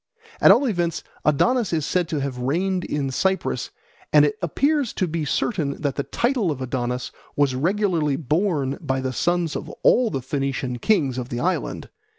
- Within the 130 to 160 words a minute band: No, average, 175 wpm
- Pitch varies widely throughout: Yes, wide, 5.9 semitones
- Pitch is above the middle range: No, medium, 150 Hz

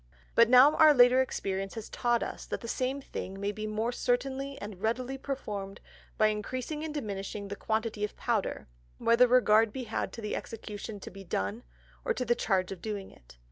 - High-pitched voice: Yes, high, 225 Hz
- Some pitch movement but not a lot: Yes, average, 3.8 semitones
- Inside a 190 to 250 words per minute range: Yes, average, 195 wpm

